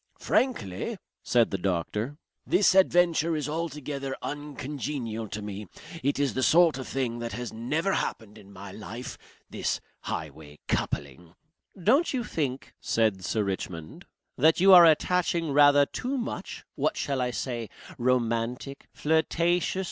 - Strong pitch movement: Yes, wide, 6.6 semitones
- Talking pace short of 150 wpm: Yes, average, 140 wpm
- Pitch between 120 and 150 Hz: Yes, low, 135 Hz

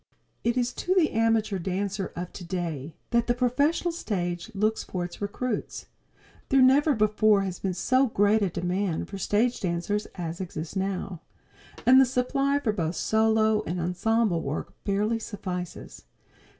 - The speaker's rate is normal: Yes, average, 150 wpm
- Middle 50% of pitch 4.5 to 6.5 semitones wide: Yes, average, 4.8 semitones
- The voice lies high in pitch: Yes, high, 205 Hz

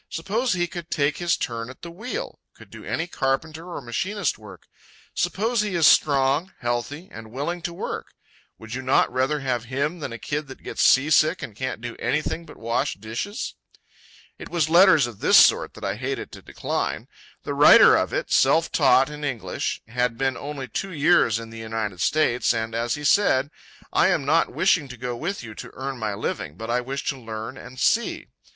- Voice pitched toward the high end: No, low, 135 Hz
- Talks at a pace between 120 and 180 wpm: No, average, 200 wpm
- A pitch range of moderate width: No, wide, 5.7 semitones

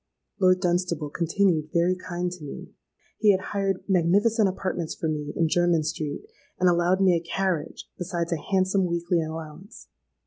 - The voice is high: No, medium, 175 Hz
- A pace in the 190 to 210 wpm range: No, average, 160 wpm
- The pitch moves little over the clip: Yes, narrow, 2.3 semitones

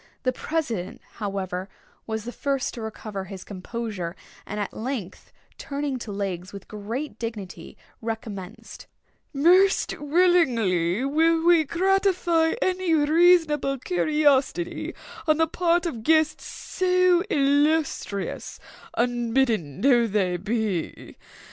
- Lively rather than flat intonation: Yes, wide, 7.8 semitones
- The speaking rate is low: Yes, slow, 110 wpm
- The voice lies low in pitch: No, very high, 255 Hz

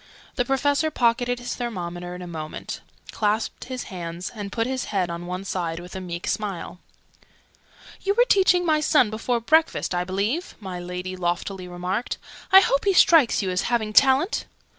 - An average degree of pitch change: No, wide, 6.5 semitones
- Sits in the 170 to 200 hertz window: No, high, 210 Hz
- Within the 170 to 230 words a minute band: Yes, average, 175 wpm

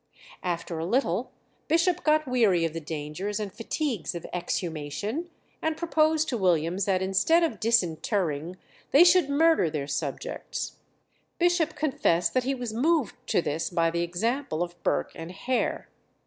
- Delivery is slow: No, average, 150 wpm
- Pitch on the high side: Yes, high, 205 Hz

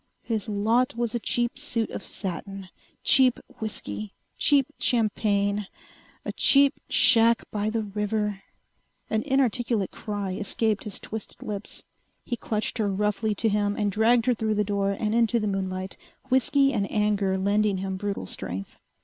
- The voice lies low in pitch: No, high, 210 Hz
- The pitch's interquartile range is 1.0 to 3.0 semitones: Yes, narrow, 2.5 semitones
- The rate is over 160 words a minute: No, average, 150 wpm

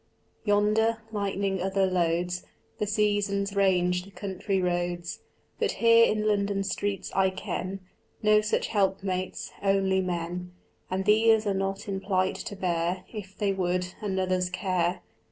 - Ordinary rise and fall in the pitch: No, narrow, 2.0 semitones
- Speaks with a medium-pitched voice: No, high, 195 Hz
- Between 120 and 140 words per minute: Yes, slow, 135 wpm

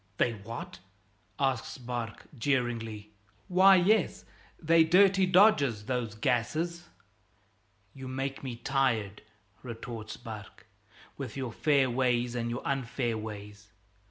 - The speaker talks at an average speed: No, slow, 115 wpm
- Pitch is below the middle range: Yes, low, 125 Hz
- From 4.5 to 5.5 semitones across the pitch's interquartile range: No, average, 3.9 semitones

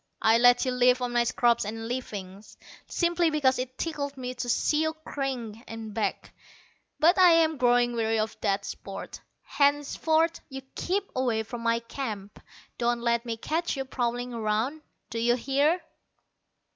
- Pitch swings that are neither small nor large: Yes, average, 3.9 semitones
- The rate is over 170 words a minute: No, average, 160 wpm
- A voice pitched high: Yes, high, 245 Hz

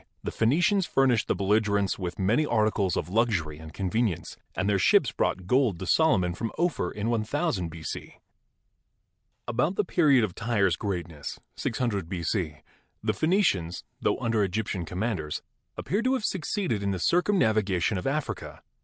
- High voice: No, low, 105 Hz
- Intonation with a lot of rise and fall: Yes, wide, 6.4 semitones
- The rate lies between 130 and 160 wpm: Yes, average, 150 wpm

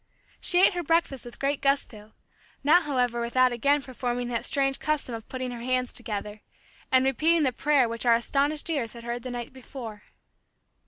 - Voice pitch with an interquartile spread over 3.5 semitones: No, average, 3.1 semitones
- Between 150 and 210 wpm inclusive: Yes, average, 180 wpm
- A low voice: No, very high, 255 Hz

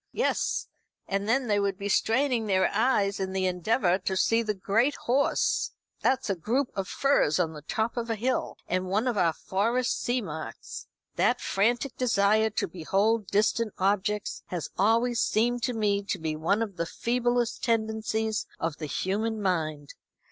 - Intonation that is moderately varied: Yes, average, 3.6 semitones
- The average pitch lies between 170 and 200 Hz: No, high, 210 Hz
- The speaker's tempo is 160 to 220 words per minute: Yes, average, 170 wpm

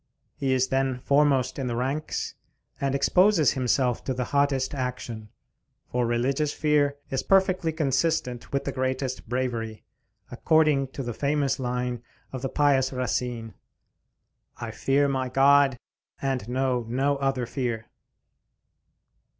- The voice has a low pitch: Yes, low, 130 Hz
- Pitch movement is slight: Yes, narrow, 2.2 semitones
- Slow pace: Yes, slow, 130 wpm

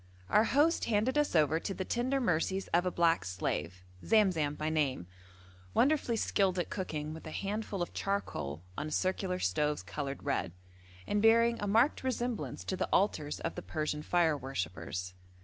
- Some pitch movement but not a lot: No, wide, 6.2 semitones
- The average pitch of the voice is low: No, medium, 180 Hz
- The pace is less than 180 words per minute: Yes, average, 165 wpm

